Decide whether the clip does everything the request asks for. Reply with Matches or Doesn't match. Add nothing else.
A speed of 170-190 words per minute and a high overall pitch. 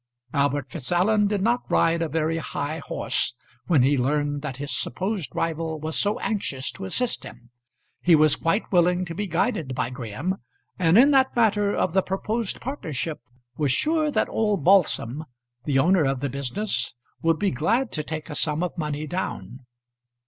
Doesn't match